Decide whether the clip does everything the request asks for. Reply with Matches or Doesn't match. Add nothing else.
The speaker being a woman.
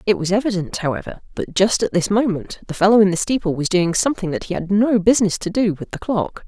Matches